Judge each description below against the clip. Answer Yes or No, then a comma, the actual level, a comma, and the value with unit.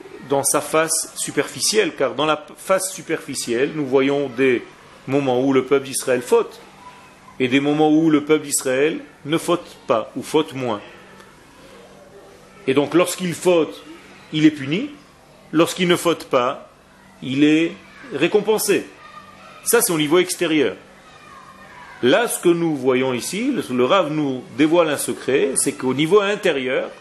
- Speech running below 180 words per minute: Yes, slow, 145 wpm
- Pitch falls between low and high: Yes, medium, 155 Hz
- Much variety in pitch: No, average, 4.1 semitones